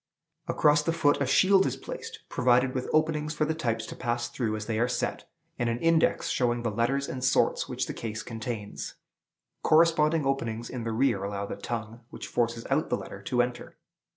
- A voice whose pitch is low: Yes, low, 125 Hz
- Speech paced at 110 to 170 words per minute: No, average, 200 wpm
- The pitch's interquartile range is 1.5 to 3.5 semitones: No, average, 4.4 semitones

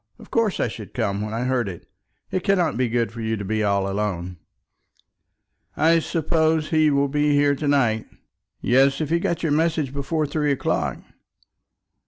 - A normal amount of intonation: No, wide, 6.1 semitones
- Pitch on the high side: No, medium, 140 Hz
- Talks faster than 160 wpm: Yes, average, 180 wpm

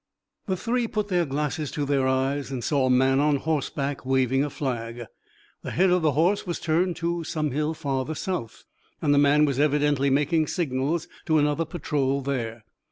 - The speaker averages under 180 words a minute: No, average, 185 wpm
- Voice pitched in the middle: Yes, medium, 145 Hz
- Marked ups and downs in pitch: No, average, 3.3 semitones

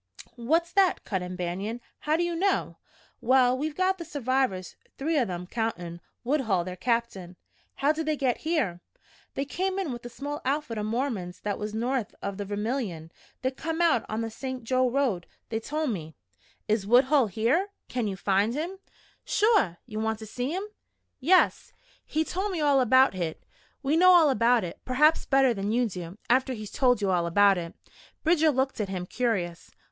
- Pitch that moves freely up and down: Yes, wide, 6.6 semitones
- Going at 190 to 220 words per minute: Yes, average, 195 wpm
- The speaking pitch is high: Yes, high, 245 Hz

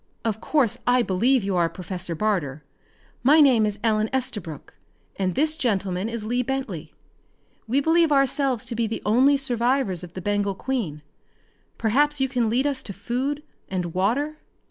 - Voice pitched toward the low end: No, high, 230 Hz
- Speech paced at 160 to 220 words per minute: Yes, average, 165 wpm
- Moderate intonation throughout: No, wide, 5.7 semitones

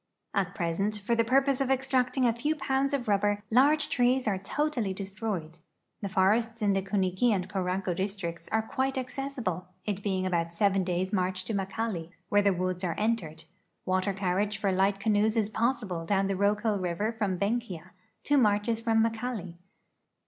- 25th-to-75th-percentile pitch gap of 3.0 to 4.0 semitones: Yes, average, 3.7 semitones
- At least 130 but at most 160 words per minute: No, average, 180 wpm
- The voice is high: Yes, high, 205 Hz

